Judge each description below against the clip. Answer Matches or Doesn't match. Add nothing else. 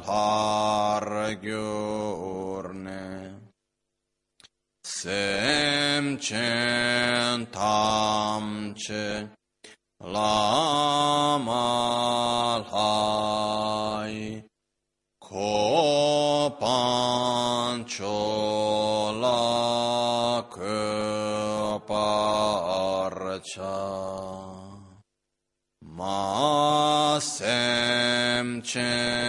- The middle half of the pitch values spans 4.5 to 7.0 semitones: Doesn't match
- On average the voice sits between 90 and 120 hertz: Matches